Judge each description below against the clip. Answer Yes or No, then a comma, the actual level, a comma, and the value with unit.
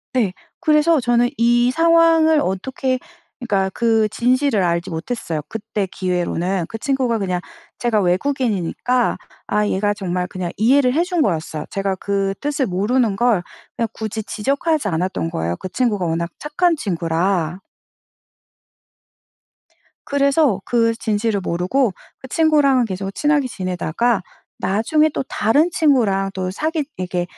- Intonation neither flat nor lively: No, wide, 6.3 semitones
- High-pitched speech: Yes, high, 220 Hz